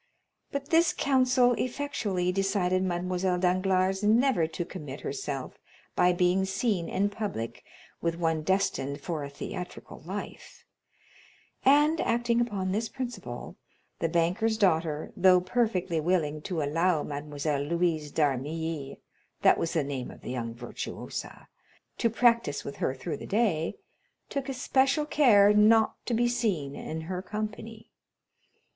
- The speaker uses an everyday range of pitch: No, wide, 6.0 semitones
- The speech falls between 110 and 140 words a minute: Yes, slow, 135 wpm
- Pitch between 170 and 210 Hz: Yes, medium, 185 Hz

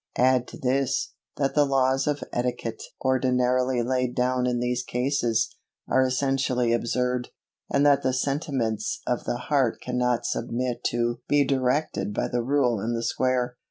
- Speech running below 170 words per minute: Yes, average, 155 wpm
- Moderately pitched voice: No, low, 125 Hz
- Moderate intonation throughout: No, narrow, 1.5 semitones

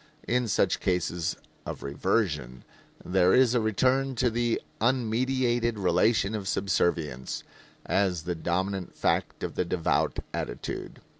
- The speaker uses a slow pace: Yes, slow, 125 wpm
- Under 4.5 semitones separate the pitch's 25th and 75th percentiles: No, average, 5.0 semitones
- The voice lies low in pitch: Yes, low, 100 Hz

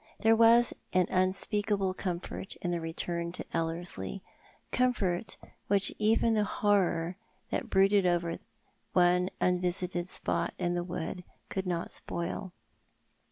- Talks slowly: Yes, slow, 115 wpm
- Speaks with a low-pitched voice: No, medium, 180 Hz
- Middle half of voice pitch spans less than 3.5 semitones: Yes, narrow, 2.4 semitones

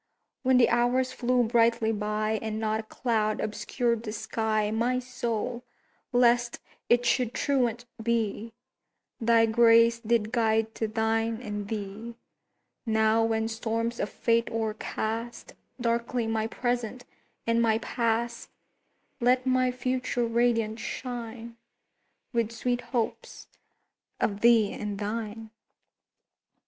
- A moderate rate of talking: No, slow, 115 wpm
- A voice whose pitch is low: No, high, 230 Hz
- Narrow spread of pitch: Yes, narrow, 1.5 semitones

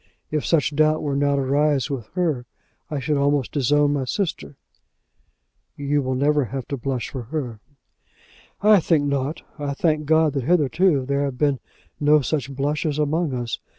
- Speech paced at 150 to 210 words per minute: Yes, average, 170 wpm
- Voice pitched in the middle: Yes, medium, 145 Hz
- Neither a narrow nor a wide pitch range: No, narrow, 2.1 semitones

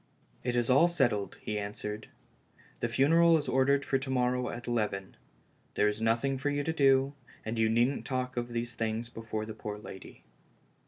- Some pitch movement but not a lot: Yes, average, 3.5 semitones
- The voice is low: Yes, low, 120 Hz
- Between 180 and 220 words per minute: Yes, average, 190 wpm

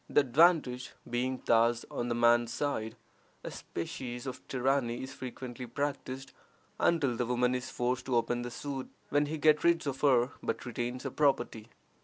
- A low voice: Yes, low, 125 Hz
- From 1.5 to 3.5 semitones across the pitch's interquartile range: Yes, narrow, 2.5 semitones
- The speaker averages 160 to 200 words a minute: Yes, average, 170 wpm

